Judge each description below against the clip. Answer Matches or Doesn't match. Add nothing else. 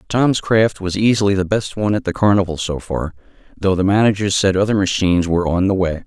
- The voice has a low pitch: Matches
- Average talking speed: Doesn't match